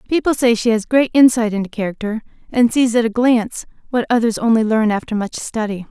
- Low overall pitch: No, high, 230 Hz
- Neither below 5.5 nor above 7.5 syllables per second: Yes, 5.9 syllables/s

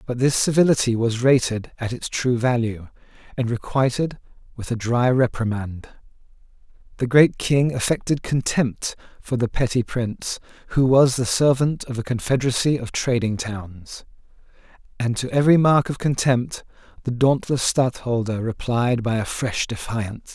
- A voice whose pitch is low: Yes, low, 125 Hz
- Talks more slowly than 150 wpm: Yes, average, 140 wpm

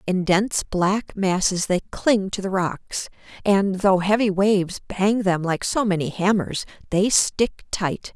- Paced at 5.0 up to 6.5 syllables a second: No, 4.0 syllables/s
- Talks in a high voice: Yes, high, 195 Hz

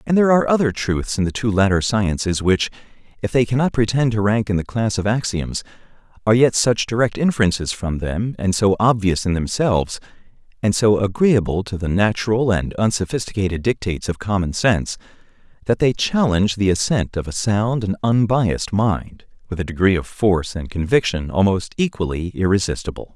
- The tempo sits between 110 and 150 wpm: No, average, 175 wpm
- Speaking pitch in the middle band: No, low, 105 Hz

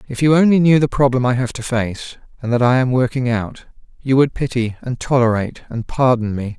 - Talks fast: Yes, fast, 220 wpm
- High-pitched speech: No, low, 125 Hz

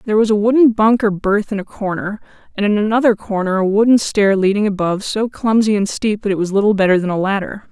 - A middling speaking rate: No, fast, 235 wpm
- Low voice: No, high, 205 Hz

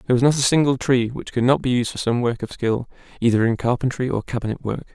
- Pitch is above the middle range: No, low, 125 Hz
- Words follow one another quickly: Yes, fast, 265 wpm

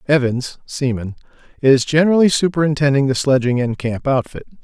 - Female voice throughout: No, male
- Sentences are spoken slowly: Yes, slow, 130 wpm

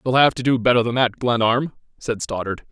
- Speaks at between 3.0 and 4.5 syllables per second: No, 5.6 syllables/s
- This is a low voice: Yes, low, 120 Hz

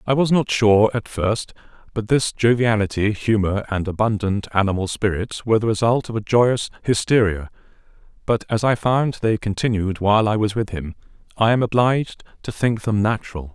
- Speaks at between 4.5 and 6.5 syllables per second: Yes, 5.2 syllables/s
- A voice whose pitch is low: Yes, low, 110 Hz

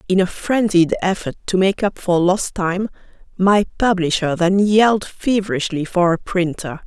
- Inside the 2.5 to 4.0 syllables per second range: No, 4.6 syllables/s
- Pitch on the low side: No, medium, 185 Hz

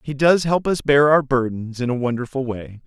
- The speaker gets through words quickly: Yes, fast, 230 wpm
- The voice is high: No, low, 135 Hz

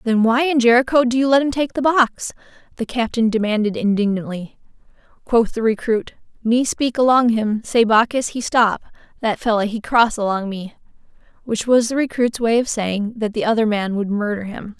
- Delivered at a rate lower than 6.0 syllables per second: Yes, 5.1 syllables/s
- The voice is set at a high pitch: Yes, high, 230 Hz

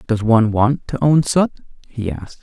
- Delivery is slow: No, average, 200 wpm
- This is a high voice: No, low, 120 Hz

